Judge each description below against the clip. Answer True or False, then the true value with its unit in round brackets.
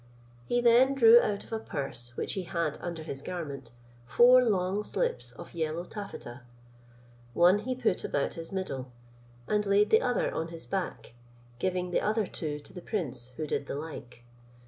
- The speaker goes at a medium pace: True (175 wpm)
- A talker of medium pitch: True (180 Hz)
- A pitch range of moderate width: False (5.8 semitones)